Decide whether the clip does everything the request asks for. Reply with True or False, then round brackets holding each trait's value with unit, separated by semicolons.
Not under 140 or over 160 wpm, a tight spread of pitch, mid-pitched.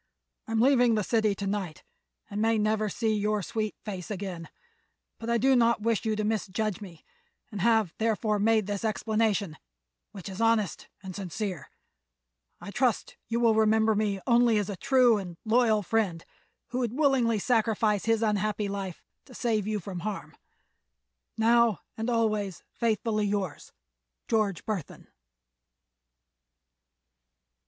False (145 wpm; 2.2 semitones; 215 Hz)